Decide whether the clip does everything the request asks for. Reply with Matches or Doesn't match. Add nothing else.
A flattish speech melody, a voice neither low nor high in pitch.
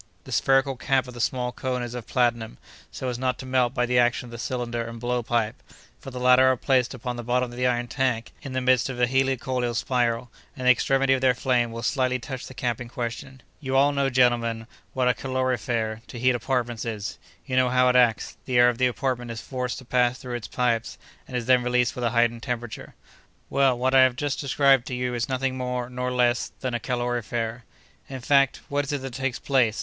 Doesn't match